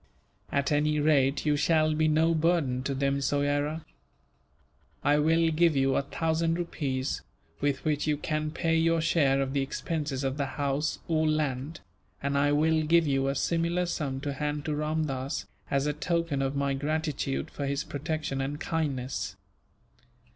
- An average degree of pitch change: No, narrow, 2.3 semitones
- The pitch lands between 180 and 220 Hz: No, medium, 150 Hz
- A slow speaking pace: No, average, 165 wpm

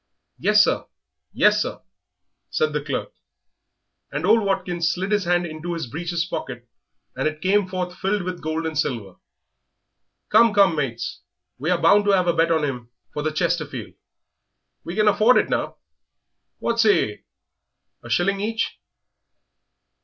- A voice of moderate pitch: Yes, medium, 175 Hz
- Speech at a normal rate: Yes, average, 155 wpm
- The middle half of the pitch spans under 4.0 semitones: No, average, 4.5 semitones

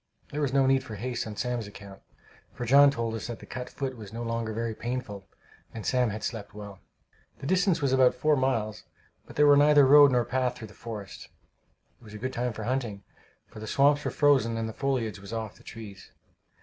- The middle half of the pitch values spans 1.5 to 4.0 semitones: Yes, average, 3.6 semitones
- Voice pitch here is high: No, low, 120 Hz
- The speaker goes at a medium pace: No, fast, 225 wpm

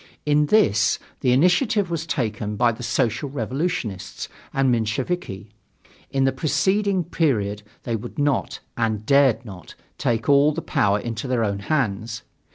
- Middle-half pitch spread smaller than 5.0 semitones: No, wide, 5.4 semitones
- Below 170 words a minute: Yes, average, 150 wpm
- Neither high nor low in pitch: No, low, 125 Hz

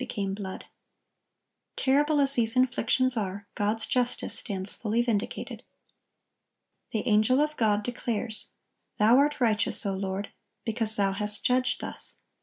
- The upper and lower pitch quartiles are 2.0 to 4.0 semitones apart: Yes, average, 3.4 semitones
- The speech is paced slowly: Yes, slow, 130 wpm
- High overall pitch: Yes, high, 220 Hz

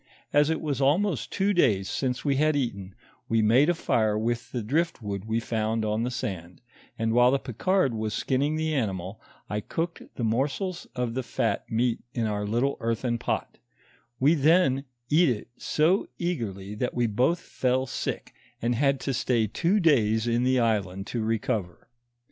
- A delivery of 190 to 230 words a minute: No, average, 175 wpm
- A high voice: No, low, 120 Hz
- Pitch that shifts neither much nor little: Yes, average, 4.7 semitones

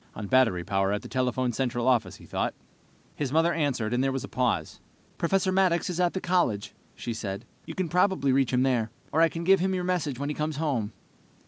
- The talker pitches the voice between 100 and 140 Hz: Yes, low, 135 Hz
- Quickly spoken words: Yes, fast, 225 wpm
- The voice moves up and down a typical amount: No, wide, 6.0 semitones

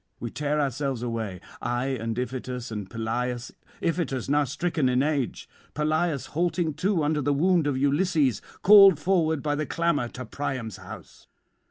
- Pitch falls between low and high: Yes, medium, 145 Hz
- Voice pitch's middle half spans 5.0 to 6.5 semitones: No, average, 4.1 semitones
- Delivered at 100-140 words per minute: No, average, 155 wpm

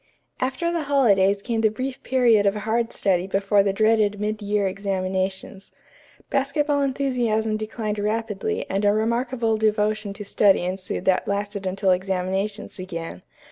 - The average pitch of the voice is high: Yes, high, 210 Hz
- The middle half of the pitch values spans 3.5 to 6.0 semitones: No, average, 2.7 semitones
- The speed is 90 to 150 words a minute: Yes, average, 140 wpm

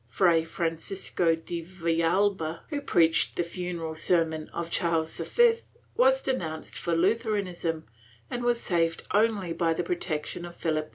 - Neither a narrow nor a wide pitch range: Yes, average, 3.1 semitones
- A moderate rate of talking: Yes, average, 145 wpm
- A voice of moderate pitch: Yes, medium, 170 Hz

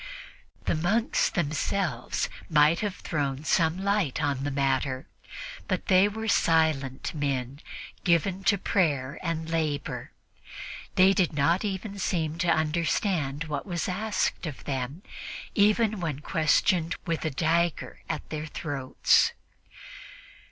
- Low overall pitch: No, medium, 160 Hz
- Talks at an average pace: No, slow, 120 wpm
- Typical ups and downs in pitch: Yes, average, 4.3 semitones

